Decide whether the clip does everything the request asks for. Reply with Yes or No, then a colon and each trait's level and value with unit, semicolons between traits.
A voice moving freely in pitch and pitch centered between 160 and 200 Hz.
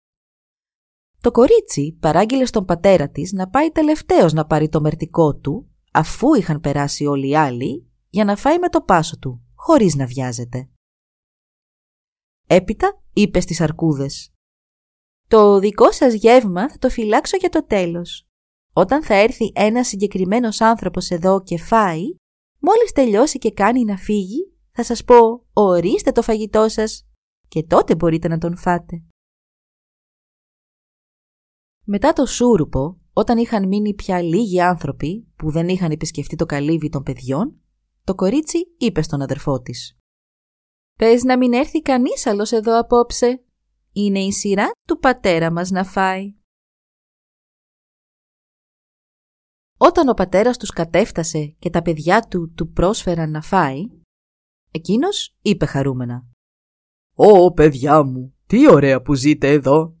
Yes: wide, 6.8 semitones; medium, 185 Hz